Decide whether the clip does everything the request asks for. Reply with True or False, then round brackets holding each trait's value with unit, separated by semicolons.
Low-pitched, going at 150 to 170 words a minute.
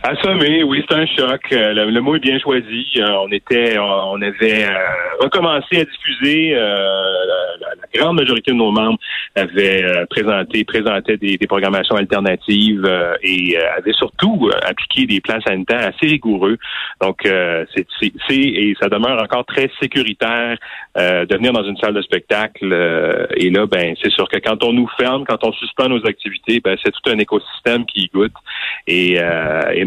False (110 Hz; 190 wpm)